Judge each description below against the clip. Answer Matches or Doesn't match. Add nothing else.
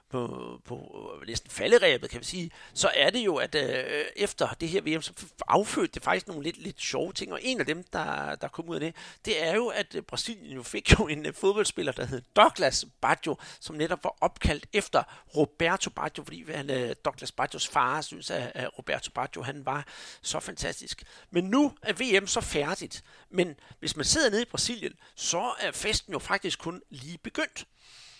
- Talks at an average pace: Matches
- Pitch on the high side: Matches